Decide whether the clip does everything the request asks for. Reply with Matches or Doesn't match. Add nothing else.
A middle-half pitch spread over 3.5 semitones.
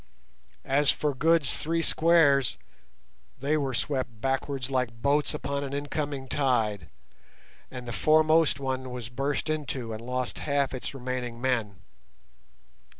Doesn't match